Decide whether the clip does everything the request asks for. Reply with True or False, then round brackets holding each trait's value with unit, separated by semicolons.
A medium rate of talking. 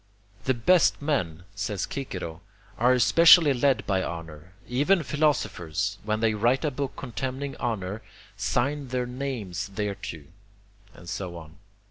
False (130 wpm)